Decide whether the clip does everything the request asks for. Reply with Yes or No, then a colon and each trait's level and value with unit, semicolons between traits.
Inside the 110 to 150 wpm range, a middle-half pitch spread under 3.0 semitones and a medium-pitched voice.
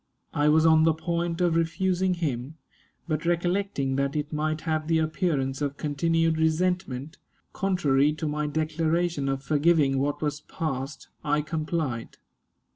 Yes: average, 140 wpm; narrow, 2.5 semitones; medium, 155 Hz